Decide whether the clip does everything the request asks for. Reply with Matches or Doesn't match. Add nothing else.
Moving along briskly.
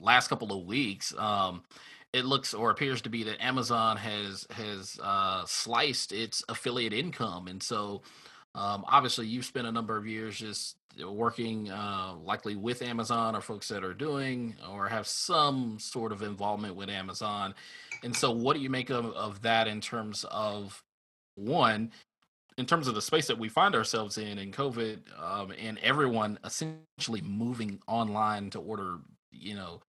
Doesn't match